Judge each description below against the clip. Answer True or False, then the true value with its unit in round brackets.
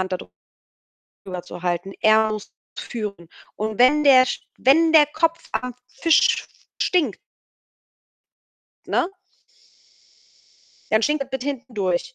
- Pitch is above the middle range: True (245 Hz)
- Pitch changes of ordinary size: False (6.7 semitones)